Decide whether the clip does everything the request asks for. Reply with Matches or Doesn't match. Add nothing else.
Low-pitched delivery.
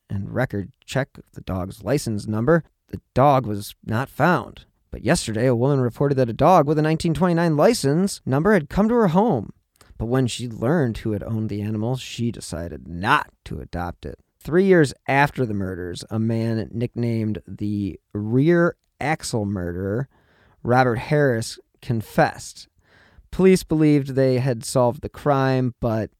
Matches